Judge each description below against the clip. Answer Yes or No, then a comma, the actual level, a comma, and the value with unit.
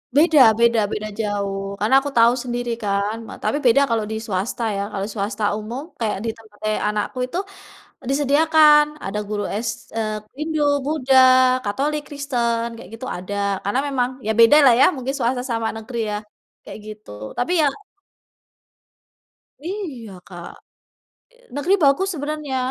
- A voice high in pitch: Yes, high, 235 Hz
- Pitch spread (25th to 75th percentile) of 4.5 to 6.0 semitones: Yes, average, 5.0 semitones